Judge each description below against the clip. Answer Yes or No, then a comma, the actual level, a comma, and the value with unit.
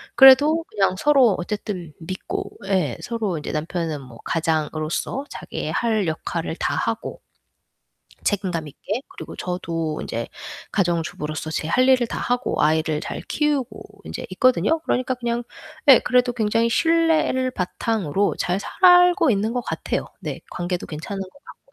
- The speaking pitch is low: No, high, 205 Hz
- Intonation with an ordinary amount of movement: No, wide, 7.5 semitones